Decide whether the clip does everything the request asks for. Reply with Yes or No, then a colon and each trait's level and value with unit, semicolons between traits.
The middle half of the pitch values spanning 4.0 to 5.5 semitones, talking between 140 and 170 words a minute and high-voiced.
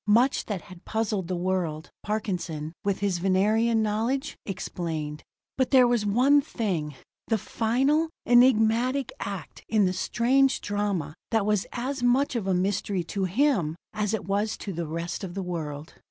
Yes: average, 4.8 semitones; average, 160 wpm; high, 205 Hz